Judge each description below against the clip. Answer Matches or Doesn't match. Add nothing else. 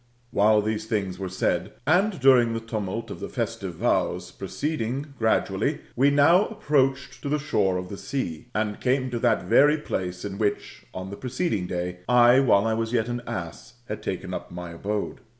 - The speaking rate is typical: Matches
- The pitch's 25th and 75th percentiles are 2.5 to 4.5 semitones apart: Doesn't match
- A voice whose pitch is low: Matches